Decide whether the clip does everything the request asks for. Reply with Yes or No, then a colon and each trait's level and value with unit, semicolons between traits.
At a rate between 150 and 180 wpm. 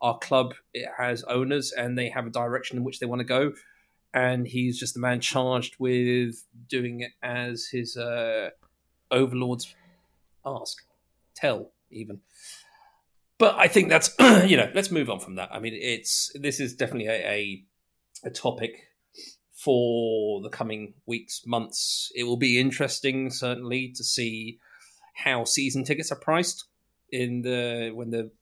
Yes: average, 155 wpm